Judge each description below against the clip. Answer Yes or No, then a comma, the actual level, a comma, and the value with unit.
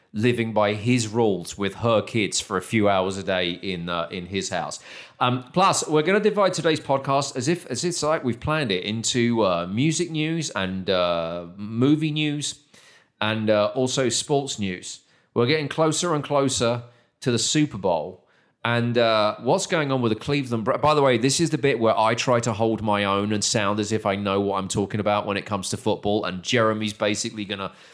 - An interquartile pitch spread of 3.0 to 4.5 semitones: No, wide, 5.4 semitones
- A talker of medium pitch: No, low, 115 Hz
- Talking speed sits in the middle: No, fast, 210 wpm